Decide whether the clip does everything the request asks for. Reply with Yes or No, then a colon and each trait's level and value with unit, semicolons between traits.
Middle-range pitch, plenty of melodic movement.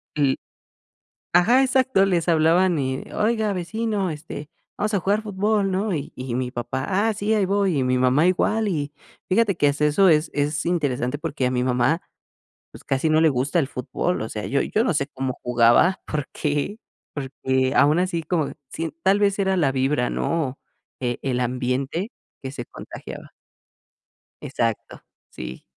Yes: medium, 155 Hz; wide, 6.5 semitones